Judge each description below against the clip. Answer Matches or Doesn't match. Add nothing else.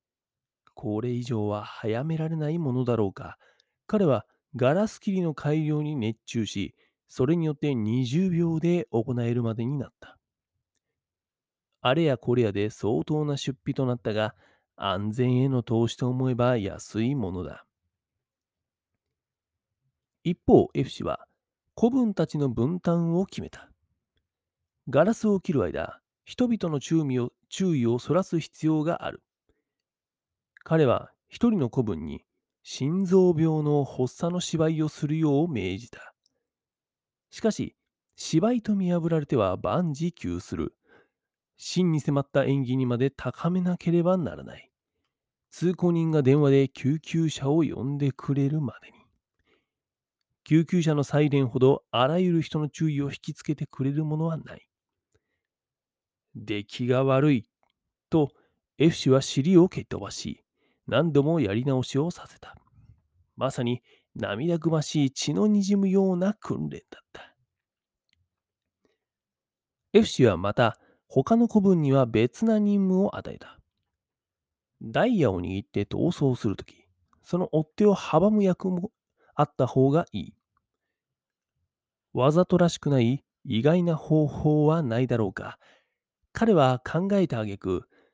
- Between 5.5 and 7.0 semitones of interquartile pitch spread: Matches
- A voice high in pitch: Doesn't match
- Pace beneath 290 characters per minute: Matches